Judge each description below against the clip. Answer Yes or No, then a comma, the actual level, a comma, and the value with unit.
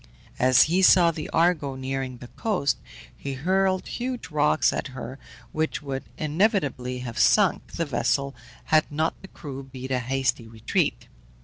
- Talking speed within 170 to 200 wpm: No, average, 150 wpm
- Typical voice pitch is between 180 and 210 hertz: No, medium, 140 Hz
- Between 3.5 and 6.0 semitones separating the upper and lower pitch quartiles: Yes, average, 4.3 semitones